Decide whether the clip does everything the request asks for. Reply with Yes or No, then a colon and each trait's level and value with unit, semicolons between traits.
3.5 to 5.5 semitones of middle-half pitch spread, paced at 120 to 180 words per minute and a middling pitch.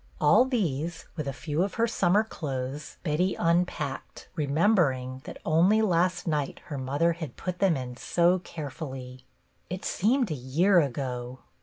Yes: average, 5.2 semitones; average, 155 wpm; medium, 160 Hz